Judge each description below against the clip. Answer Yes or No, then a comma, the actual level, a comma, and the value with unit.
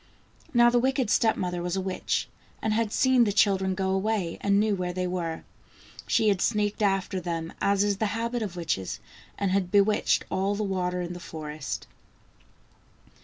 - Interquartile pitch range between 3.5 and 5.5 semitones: No, average, 2.9 semitones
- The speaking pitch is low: No, high, 195 Hz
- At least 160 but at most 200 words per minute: Yes, average, 180 wpm